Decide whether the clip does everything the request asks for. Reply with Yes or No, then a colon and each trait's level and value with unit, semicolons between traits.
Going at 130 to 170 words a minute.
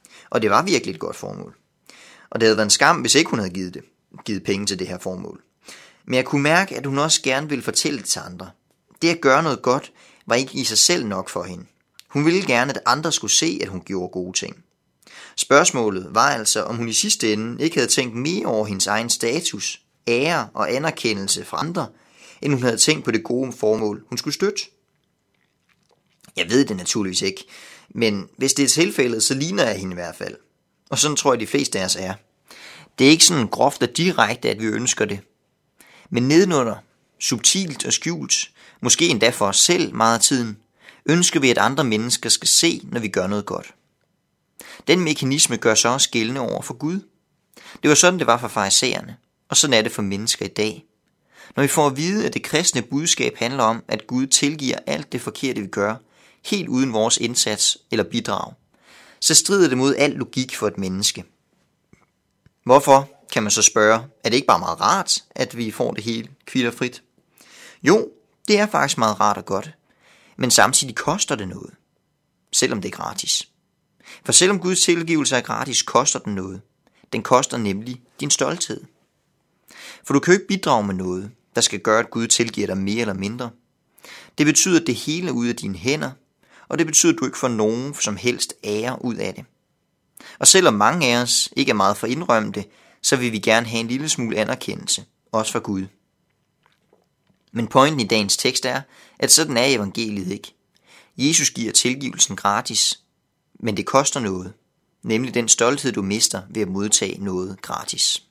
No: average, 195 wpm